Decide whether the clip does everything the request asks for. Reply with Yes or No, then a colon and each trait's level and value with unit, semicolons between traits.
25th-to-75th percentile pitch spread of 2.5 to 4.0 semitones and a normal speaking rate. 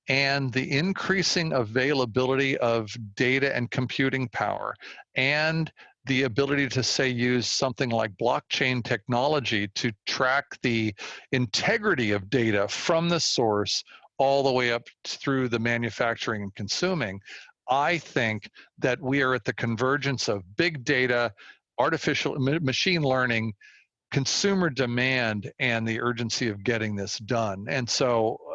No: average, 3.1 semitones; slow, 130 wpm